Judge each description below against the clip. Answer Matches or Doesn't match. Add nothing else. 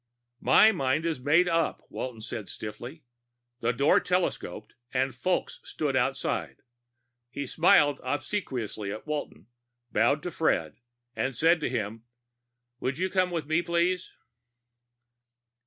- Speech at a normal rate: Doesn't match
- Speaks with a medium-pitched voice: Matches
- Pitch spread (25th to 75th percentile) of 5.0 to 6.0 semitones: Matches